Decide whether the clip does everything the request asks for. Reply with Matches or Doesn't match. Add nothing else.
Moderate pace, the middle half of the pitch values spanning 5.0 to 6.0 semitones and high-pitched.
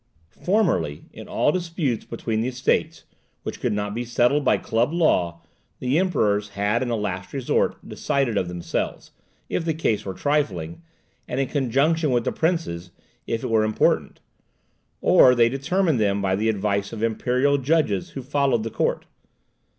Doesn't match